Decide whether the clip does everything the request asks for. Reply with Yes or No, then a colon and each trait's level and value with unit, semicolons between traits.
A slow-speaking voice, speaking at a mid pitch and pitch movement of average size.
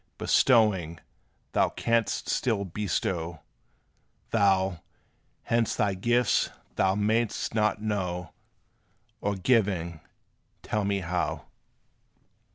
No: slow, 85 wpm; low, 100 Hz; average, 3.3 semitones